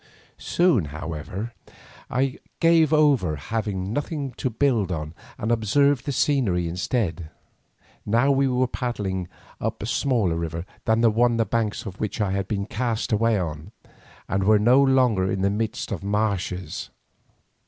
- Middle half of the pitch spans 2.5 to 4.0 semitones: No, average, 5.1 semitones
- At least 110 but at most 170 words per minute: Yes, average, 155 wpm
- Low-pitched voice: Yes, low, 110 Hz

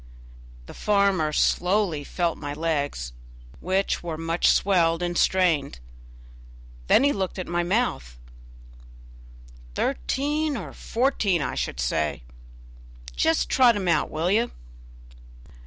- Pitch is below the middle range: No, medium, 175 Hz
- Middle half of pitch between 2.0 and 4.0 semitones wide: No, average, 4.6 semitones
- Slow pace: Yes, slow, 115 wpm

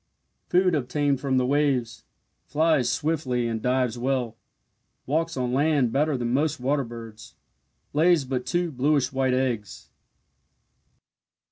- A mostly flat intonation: No, average, 3.3 semitones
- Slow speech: Yes, slow, 125 wpm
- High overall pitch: No, low, 135 Hz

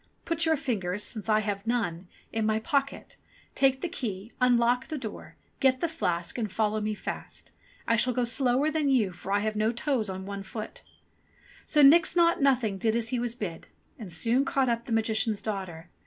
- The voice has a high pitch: Yes, high, 230 Hz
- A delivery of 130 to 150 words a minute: No, average, 200 wpm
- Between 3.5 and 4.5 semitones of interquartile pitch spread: Yes, average, 4.1 semitones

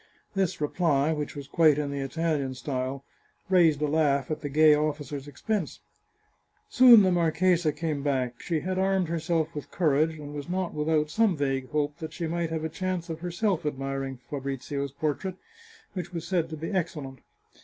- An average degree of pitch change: Yes, average, 3.3 semitones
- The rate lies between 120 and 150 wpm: No, average, 175 wpm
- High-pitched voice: No, medium, 155 Hz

